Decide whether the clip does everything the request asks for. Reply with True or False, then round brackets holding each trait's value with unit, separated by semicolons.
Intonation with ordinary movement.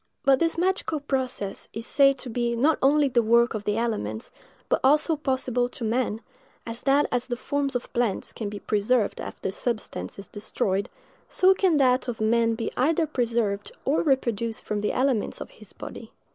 True (3.8 semitones)